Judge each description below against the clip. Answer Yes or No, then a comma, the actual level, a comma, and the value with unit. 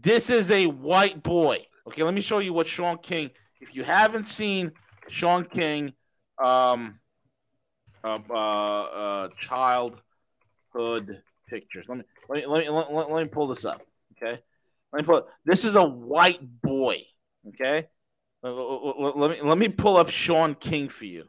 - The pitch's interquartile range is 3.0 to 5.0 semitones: No, wide, 5.5 semitones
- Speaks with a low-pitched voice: No, medium, 150 Hz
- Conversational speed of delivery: Yes, average, 170 wpm